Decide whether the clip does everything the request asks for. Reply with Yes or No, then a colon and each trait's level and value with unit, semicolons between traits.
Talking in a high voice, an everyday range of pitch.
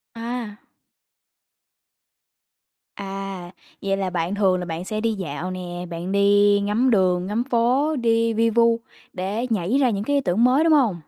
Yes: high, 205 Hz; average, 4.0 semitones